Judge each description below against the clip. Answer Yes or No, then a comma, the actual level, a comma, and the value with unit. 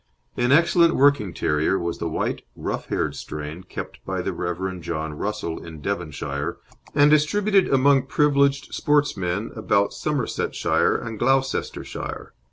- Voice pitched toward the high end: No, low, 110 Hz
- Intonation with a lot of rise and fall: Yes, wide, 9.0 semitones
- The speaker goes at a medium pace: No, slow, 130 wpm